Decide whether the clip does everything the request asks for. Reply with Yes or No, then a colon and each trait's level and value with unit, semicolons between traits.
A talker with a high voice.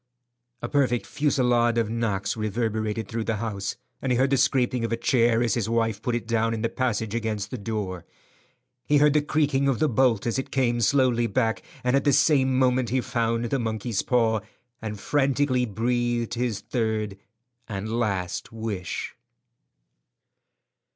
No: low, 115 Hz